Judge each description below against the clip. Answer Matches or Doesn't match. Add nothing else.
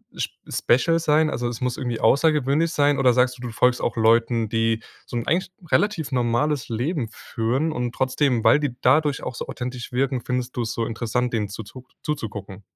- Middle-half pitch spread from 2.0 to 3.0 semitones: Doesn't match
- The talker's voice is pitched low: Matches